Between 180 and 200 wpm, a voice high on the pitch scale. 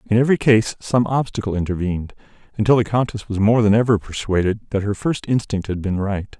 No: average, 195 wpm; low, 105 Hz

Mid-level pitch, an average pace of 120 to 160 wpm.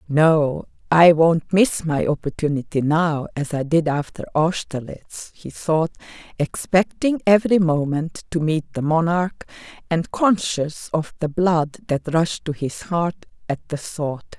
Yes: medium, 160 Hz; average, 140 wpm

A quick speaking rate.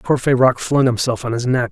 Yes: fast, 210 wpm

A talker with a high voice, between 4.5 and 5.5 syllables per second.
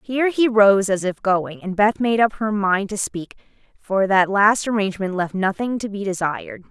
Yes: high, 205 Hz; 4.9 syllables/s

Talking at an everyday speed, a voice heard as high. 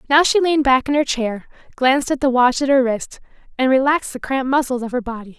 No: fast, 245 wpm; very high, 265 Hz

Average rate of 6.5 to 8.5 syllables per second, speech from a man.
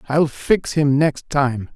No: 3.3 syllables/s; male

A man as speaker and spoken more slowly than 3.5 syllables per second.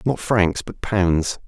Yes: male; 3.1 syllables/s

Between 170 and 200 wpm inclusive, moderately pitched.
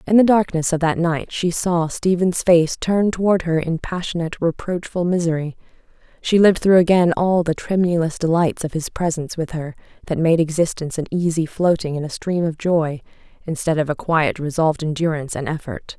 Yes: average, 185 wpm; medium, 165 Hz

